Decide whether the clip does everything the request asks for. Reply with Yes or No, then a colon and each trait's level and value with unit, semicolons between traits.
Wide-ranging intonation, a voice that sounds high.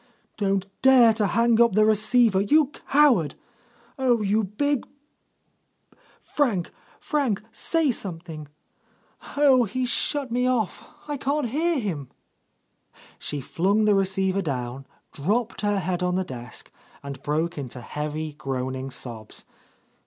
Yes: wide, 7.9 semitones; high, 200 Hz